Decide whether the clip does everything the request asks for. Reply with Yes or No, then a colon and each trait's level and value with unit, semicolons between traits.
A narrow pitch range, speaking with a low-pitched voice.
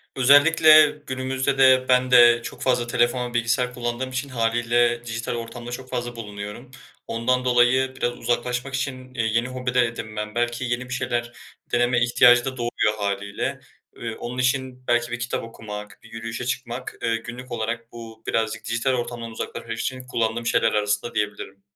Yes: narrow, 1.7 semitones; low, 120 Hz